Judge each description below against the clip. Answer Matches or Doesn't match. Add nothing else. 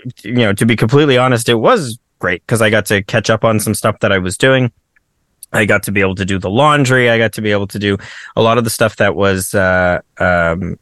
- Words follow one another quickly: Matches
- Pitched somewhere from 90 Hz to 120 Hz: Matches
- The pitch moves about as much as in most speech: Matches